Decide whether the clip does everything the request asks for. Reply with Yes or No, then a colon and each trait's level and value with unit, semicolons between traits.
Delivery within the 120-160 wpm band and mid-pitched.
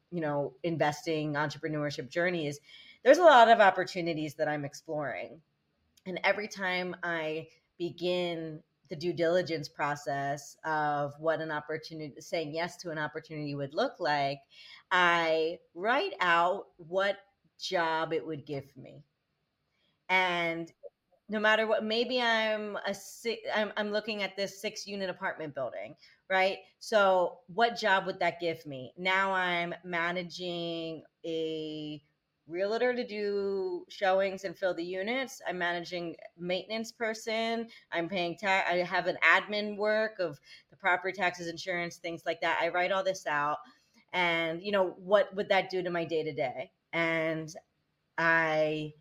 Yes: average, 145 wpm; medium, 175 Hz